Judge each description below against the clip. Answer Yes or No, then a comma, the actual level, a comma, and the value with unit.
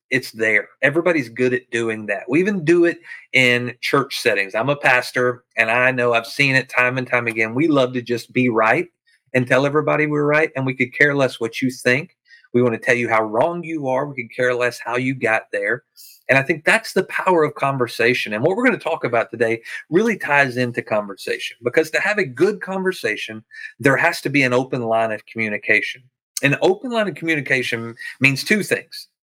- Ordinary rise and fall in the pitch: Yes, average, 3.9 semitones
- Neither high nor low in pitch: No, low, 130 Hz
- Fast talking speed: Yes, fast, 220 wpm